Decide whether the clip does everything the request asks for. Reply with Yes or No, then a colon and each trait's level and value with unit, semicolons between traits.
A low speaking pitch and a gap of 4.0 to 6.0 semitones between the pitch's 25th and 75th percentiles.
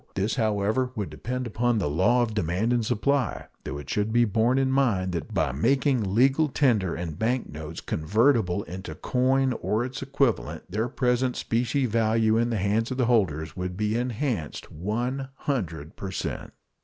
Yes: low, 115 Hz; average, 5.1 semitones